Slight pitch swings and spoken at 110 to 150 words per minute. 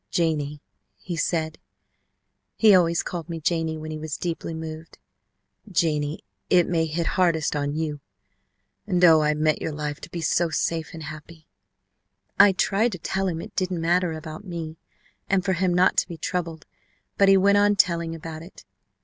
No: narrow, 2.3 semitones; average, 175 wpm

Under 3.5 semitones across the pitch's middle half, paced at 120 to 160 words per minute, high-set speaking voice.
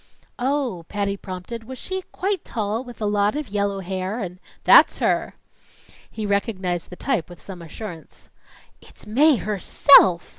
No: average, 4.6 semitones; average, 155 wpm; high, 205 Hz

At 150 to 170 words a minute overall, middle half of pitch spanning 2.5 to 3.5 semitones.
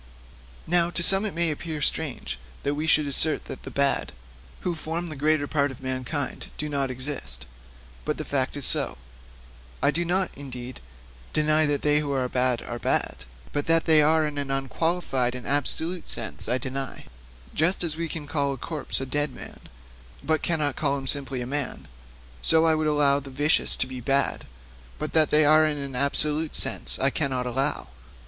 No: average, 185 wpm; average, 2.8 semitones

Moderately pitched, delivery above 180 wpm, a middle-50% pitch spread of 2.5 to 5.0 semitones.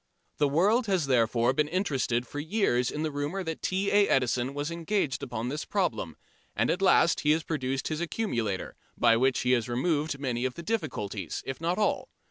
No: medium, 145 Hz; average, 195 wpm; wide, 5.5 semitones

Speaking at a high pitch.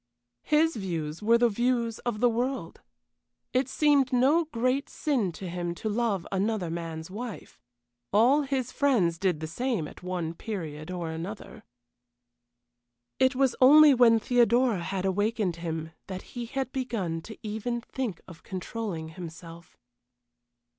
Yes: high, 220 Hz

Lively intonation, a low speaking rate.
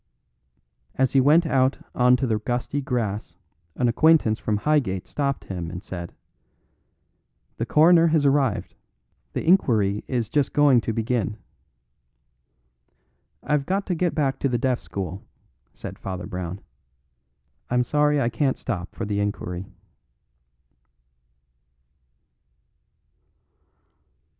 Yes: wide, 6.0 semitones; slow, 120 wpm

